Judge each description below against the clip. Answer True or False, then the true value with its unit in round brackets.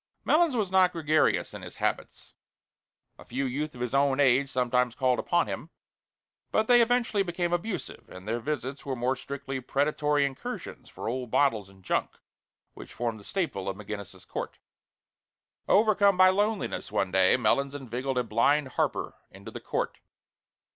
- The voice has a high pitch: False (140 Hz)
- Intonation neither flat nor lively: False (6.2 semitones)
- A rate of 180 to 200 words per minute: False (160 wpm)